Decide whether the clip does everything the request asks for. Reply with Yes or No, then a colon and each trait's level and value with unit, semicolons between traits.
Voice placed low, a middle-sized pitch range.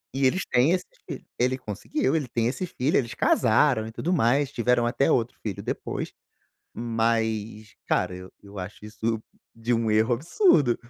Yes: low, 115 Hz; average, 3.3 semitones